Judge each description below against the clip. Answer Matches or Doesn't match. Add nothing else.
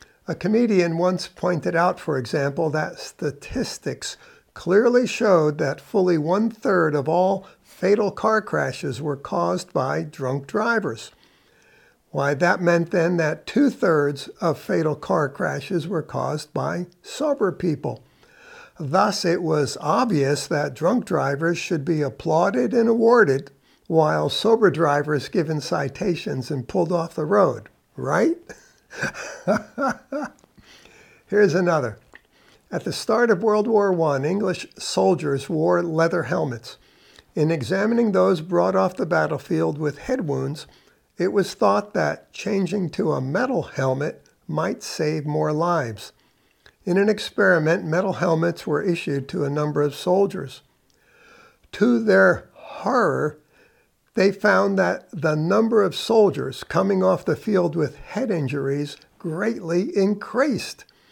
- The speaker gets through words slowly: Matches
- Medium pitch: Matches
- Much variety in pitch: Doesn't match